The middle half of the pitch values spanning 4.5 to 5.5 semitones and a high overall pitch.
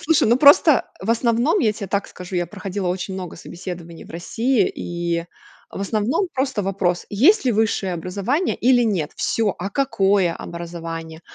Yes: average, 5.1 semitones; high, 195 Hz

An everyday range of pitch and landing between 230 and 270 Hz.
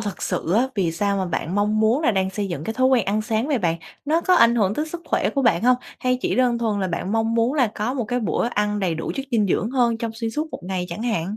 No: average, 4.2 semitones; high, 220 Hz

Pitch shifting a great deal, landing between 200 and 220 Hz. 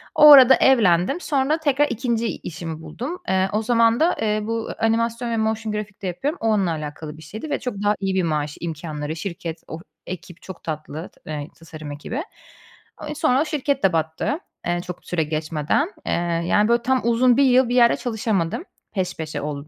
Yes: wide, 7.2 semitones; high, 210 Hz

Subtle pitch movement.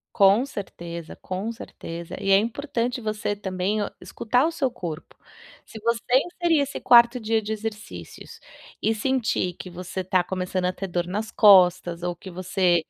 No: average, 4.2 semitones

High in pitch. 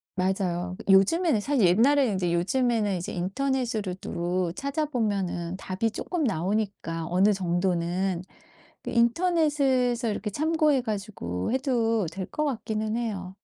Yes: high, 210 Hz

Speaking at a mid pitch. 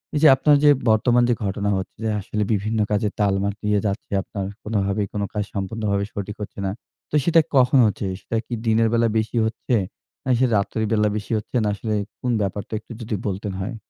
No: low, 105 Hz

